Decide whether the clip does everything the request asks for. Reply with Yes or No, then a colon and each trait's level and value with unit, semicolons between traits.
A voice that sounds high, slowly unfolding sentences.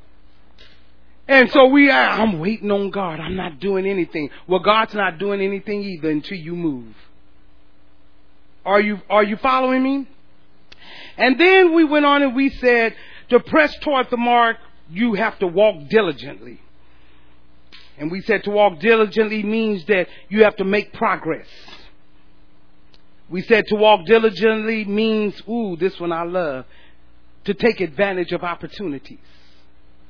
No: high, 195 Hz; average, 150 wpm